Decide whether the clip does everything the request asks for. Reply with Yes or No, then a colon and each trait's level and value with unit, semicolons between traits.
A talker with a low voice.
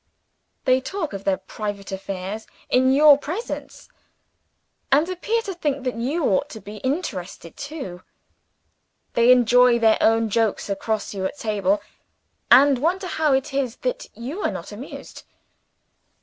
No: very high, 250 Hz